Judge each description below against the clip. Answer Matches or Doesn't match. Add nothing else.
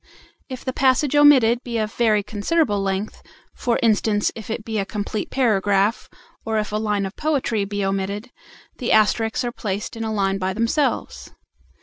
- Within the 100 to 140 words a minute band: Doesn't match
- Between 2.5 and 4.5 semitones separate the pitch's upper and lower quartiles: Matches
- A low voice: Doesn't match